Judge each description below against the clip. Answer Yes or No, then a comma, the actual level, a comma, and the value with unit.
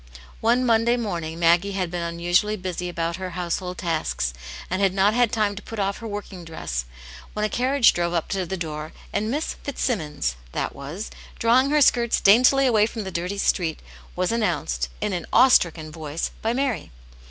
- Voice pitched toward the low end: No, high, 190 Hz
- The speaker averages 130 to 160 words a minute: No, average, 190 wpm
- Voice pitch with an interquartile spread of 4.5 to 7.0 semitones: Yes, average, 5.1 semitones